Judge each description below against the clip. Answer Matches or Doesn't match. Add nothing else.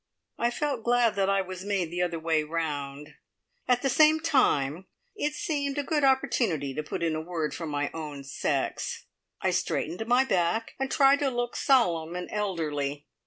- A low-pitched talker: Doesn't match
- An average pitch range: Doesn't match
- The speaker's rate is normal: Matches